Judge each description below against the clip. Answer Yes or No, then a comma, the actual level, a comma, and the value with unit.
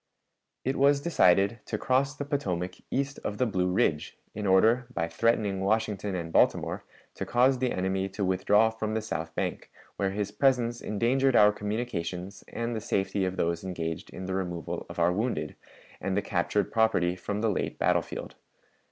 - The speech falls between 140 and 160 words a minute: No, average, 180 wpm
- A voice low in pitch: Yes, low, 105 Hz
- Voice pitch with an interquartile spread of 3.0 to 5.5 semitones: Yes, average, 4.1 semitones